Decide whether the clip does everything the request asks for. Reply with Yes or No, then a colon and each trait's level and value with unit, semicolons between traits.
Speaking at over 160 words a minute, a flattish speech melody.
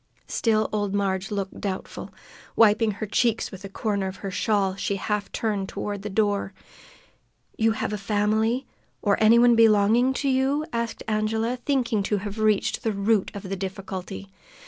Yes: average, 170 wpm; narrow, 2.3 semitones